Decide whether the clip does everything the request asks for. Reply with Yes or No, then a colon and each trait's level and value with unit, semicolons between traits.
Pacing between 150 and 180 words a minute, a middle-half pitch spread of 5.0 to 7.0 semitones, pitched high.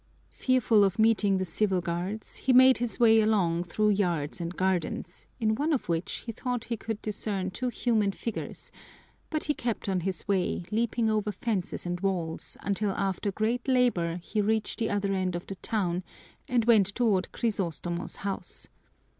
No: average, 170 wpm; average, 3.6 semitones; high, 205 Hz